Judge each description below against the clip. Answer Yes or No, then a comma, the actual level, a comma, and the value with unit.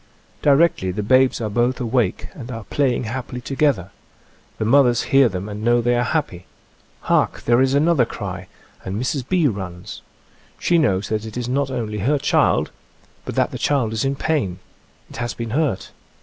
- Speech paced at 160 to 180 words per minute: No, average, 190 wpm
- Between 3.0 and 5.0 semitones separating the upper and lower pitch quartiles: Yes, average, 4.2 semitones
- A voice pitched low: Yes, low, 120 Hz